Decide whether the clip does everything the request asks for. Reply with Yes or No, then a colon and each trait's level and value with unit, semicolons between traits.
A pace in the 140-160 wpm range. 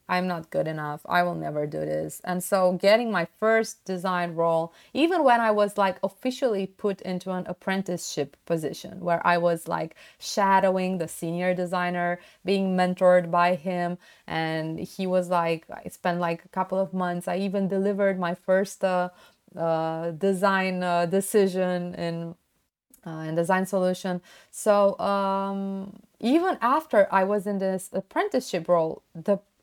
Yes: average, 155 wpm